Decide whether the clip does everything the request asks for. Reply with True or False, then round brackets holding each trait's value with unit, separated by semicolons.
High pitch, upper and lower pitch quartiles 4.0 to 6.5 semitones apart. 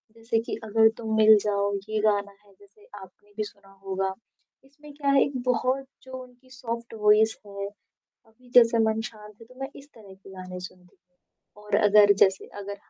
False (215 Hz; 2.8 semitones)